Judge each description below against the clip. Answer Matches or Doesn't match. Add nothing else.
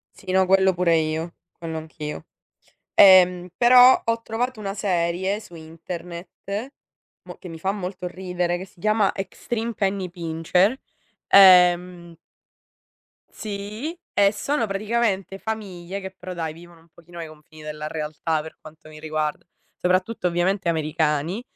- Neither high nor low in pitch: Matches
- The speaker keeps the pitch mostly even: Doesn't match